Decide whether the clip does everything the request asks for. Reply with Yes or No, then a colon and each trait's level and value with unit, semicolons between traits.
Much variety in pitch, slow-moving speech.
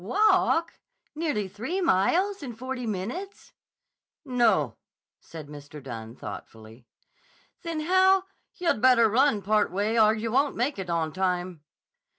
Yes: wide, 8.7 semitones; slow, 130 wpm